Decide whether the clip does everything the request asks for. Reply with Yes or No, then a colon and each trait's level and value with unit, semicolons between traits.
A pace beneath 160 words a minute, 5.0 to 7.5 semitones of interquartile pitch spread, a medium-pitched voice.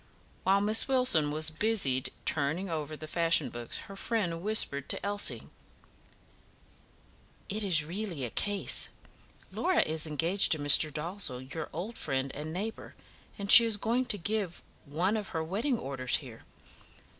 Yes: average, 150 wpm; wide, 5.6 semitones; medium, 170 Hz